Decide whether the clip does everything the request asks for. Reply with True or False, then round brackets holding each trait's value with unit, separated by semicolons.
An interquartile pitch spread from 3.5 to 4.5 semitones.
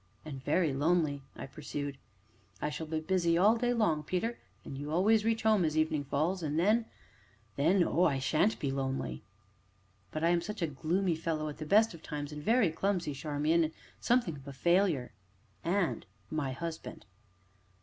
True (4.2 semitones)